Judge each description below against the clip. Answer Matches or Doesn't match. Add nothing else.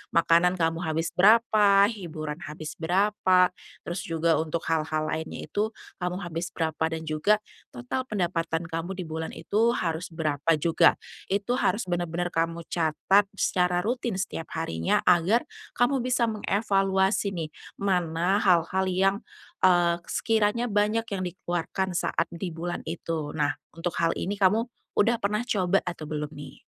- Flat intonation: Doesn't match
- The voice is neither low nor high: Matches